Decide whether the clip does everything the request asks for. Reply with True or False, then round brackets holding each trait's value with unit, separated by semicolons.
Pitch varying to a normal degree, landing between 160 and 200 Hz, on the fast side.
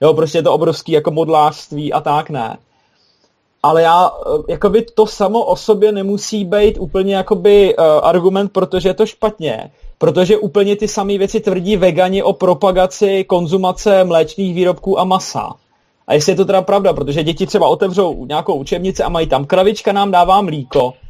True (3.6 semitones; 190 Hz; 175 wpm)